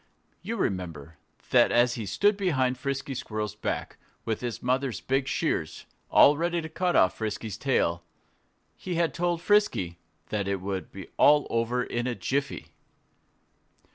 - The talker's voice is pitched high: No, low, 125 Hz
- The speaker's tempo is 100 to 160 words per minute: Yes, average, 150 wpm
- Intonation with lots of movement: Yes, wide, 6.8 semitones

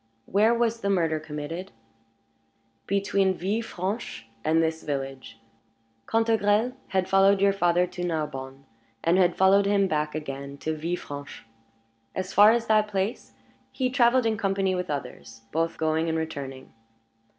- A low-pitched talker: No, medium, 180 Hz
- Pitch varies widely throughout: No, average, 4.5 semitones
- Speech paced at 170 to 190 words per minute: No, average, 140 wpm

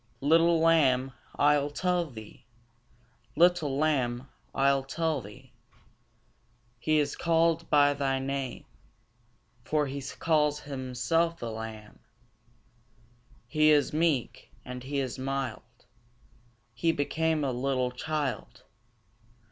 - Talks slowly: Yes, slow, 105 wpm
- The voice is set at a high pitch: No, medium, 140 Hz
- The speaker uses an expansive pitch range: No, average, 3.4 semitones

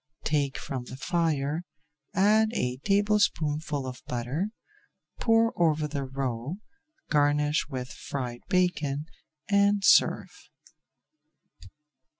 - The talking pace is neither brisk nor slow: No, slow, 95 wpm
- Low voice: No, medium, 150 Hz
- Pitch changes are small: No, average, 5.3 semitones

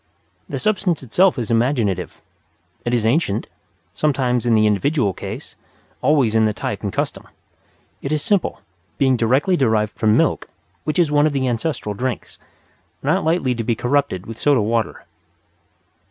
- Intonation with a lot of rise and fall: No, average, 4.9 semitones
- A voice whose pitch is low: Yes, low, 125 Hz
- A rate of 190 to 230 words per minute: No, average, 155 wpm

